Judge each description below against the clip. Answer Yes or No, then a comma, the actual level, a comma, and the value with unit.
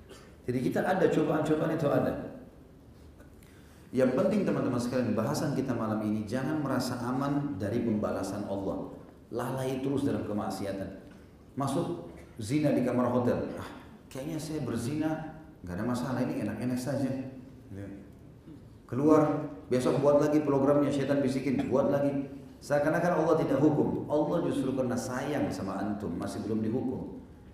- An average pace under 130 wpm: No, average, 135 wpm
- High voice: No, low, 130 Hz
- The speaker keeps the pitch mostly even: No, average, 4.7 semitones